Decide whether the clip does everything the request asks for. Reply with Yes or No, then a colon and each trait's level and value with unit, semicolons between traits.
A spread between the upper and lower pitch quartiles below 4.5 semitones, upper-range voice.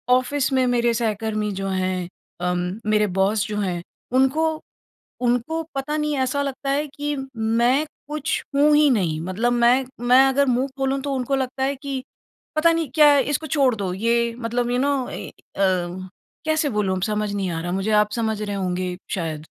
No: wide, 5.6 semitones; high, 240 Hz